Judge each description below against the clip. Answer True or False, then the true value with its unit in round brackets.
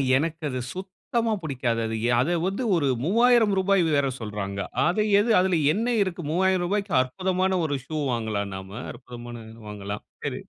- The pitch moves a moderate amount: False (7.9 semitones)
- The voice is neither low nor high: True (165 Hz)